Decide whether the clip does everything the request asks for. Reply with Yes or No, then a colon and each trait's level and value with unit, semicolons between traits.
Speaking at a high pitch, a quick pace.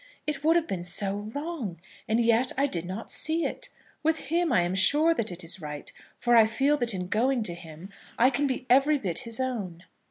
Yes: high, 230 Hz; fast, 220 wpm